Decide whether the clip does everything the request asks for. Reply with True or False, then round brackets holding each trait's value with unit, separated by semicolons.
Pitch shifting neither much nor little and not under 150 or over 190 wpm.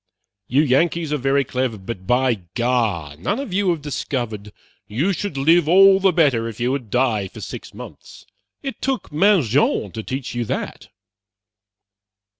False (6.5 semitones; 160 wpm)